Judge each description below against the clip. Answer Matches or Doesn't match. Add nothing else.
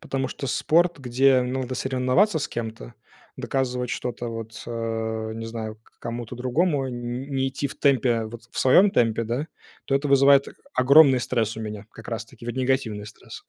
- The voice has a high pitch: Doesn't match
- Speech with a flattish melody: Doesn't match